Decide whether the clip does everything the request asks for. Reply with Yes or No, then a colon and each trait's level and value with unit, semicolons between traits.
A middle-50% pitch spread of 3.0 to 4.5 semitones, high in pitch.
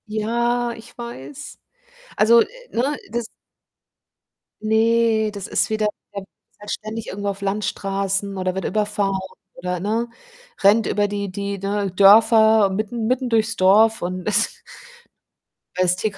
No: narrow, 2.4 semitones; high, 210 Hz